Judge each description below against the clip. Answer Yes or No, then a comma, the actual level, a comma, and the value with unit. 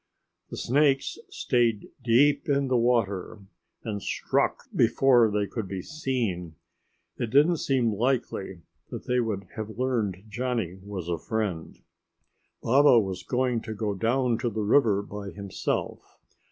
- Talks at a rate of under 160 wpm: Yes, average, 140 wpm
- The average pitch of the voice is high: No, low, 115 Hz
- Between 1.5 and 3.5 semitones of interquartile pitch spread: No, average, 4.0 semitones